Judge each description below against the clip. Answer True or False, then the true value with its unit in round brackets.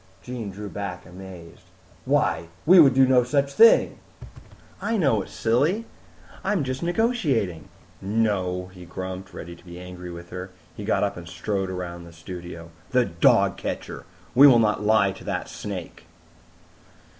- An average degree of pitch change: False (6.2 semitones)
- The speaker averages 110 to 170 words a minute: True (160 wpm)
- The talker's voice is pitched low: True (95 Hz)